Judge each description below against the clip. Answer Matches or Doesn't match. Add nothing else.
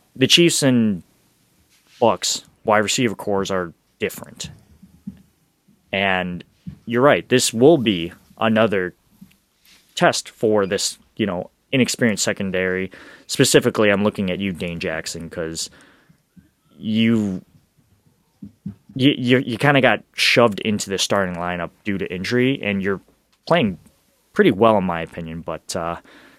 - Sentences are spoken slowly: Matches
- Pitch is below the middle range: Matches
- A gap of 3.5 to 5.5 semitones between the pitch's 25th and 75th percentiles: Matches